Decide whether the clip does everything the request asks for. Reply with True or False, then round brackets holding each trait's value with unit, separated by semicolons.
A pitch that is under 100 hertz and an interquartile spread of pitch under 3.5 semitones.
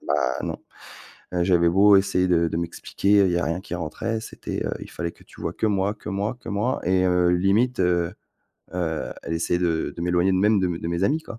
True (90 Hz; 2.9 semitones)